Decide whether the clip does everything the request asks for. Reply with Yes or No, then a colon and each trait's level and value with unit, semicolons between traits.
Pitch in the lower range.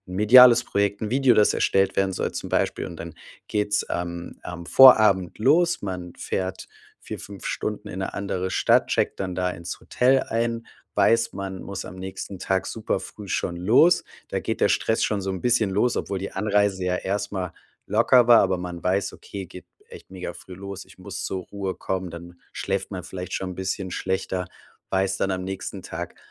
Yes: very low, 95 Hz